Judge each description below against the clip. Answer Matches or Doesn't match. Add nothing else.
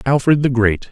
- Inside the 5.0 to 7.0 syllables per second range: Matches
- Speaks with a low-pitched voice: Matches